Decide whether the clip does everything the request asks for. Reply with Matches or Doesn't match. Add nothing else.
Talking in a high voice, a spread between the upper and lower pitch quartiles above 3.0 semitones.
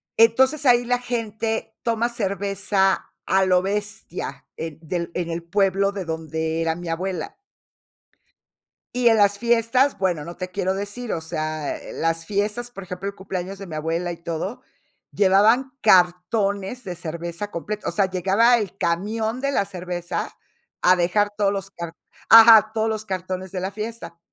Matches